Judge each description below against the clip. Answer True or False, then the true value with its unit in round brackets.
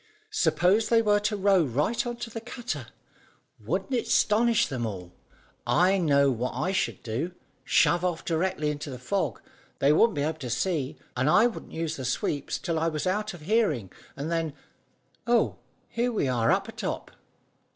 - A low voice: False (165 Hz)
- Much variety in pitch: True (7.1 semitones)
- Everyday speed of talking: True (180 wpm)